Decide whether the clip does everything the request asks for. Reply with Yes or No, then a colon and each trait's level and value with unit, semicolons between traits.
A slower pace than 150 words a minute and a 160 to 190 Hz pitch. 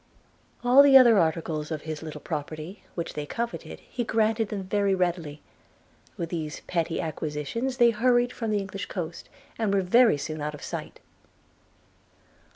No: average, 160 wpm; medium, 185 Hz